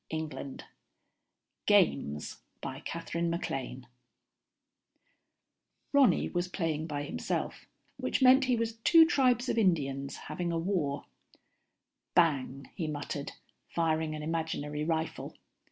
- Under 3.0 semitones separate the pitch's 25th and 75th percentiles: No, average, 4.2 semitones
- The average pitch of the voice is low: No, medium, 165 Hz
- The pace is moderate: No, slow, 100 wpm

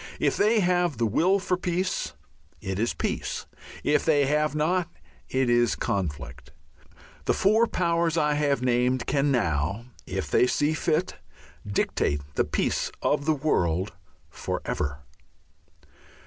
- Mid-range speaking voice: Yes, medium, 145 Hz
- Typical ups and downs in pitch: No, wide, 7.6 semitones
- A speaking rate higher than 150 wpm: No, slow, 135 wpm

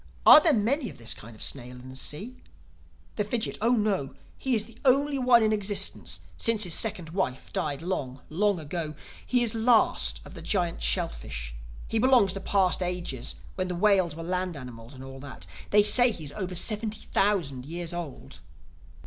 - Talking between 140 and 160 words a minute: No, average, 190 wpm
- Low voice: No, medium, 185 Hz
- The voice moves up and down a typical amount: No, wide, 7.3 semitones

